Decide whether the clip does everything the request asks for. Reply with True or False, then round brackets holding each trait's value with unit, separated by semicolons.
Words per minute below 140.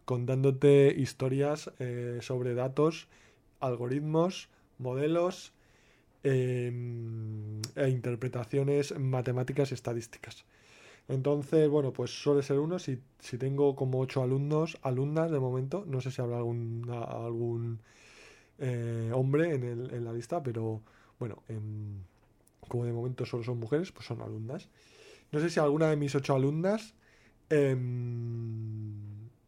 True (130 wpm)